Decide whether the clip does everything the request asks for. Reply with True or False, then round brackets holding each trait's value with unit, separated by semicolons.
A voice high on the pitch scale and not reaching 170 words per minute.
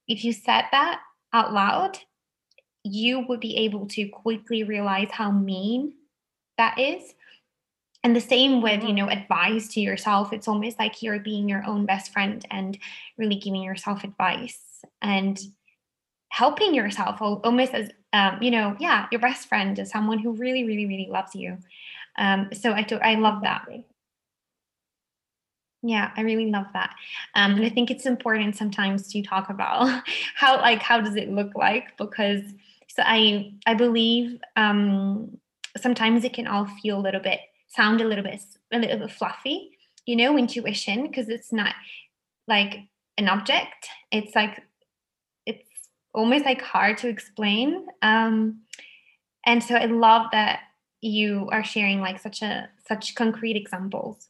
True (220 Hz; 160 wpm)